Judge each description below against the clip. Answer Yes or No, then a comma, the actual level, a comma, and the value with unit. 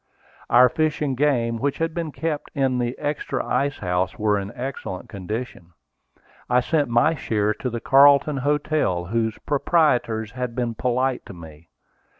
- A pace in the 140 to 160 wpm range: Yes, average, 155 wpm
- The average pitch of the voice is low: Yes, low, 125 Hz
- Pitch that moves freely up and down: No, average, 4.5 semitones